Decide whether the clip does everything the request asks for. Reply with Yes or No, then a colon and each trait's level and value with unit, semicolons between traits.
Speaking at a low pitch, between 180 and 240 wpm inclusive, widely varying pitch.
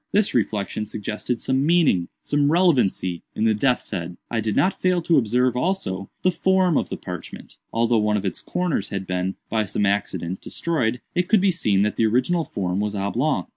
Yes: low, 115 Hz; average, 185 wpm; wide, 8.6 semitones